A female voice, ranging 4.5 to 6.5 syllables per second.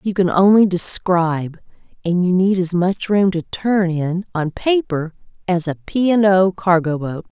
No: female; 4.3 syllables/s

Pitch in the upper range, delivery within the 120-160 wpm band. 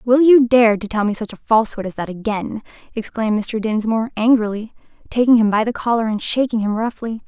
No: high, 225 Hz; fast, 205 wpm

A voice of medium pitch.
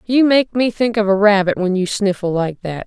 No: high, 205 Hz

